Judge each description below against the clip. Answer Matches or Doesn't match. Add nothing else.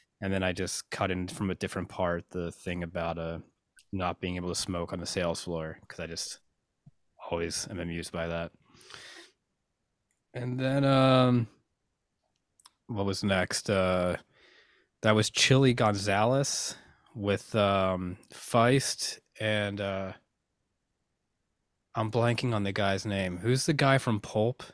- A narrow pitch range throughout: Doesn't match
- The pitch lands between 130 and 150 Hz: Doesn't match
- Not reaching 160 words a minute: Matches